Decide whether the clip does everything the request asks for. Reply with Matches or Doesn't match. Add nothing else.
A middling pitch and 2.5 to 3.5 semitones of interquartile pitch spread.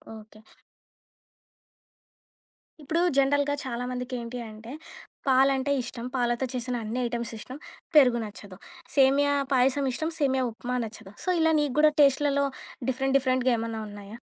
Doesn't match